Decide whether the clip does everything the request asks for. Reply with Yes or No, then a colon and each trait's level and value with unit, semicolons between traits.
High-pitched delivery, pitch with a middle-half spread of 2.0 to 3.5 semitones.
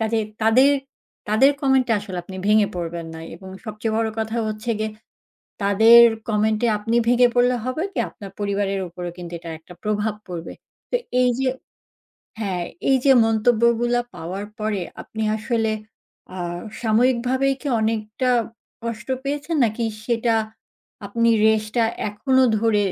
Yes: high, 220 Hz; average, 2.7 semitones